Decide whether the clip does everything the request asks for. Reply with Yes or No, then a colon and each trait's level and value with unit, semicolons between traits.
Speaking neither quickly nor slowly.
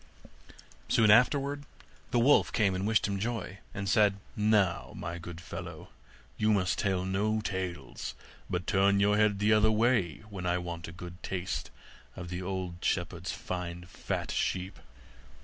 Yes: average, 155 wpm